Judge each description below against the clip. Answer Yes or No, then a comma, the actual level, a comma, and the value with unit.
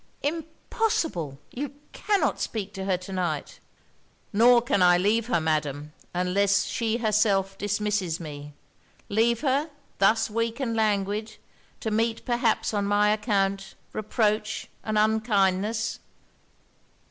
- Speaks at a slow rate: Yes, slow, 120 wpm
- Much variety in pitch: No, average, 3.0 semitones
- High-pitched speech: Yes, high, 210 Hz